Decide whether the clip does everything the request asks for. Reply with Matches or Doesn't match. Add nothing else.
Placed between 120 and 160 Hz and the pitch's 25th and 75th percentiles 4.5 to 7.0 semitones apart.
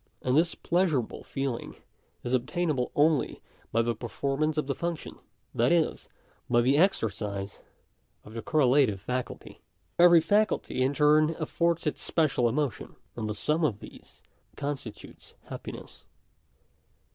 Matches